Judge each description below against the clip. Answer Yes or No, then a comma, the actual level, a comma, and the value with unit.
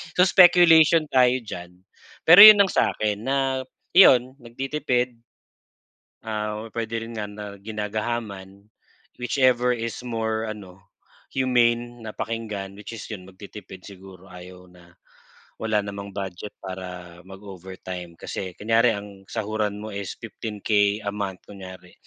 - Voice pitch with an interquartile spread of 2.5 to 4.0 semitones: Yes, average, 3.4 semitones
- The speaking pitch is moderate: No, low, 105 Hz